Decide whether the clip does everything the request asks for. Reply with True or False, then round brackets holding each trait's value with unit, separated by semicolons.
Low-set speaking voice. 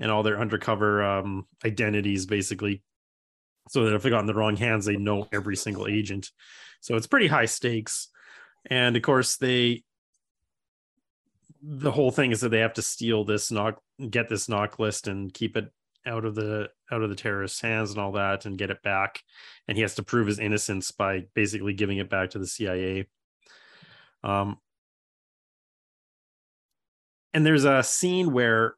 True (105 Hz)